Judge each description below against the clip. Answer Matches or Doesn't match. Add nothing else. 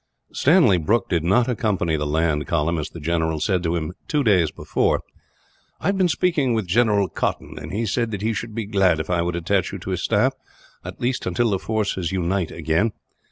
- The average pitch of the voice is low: Matches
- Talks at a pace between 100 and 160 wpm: Doesn't match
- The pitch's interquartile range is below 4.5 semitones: Doesn't match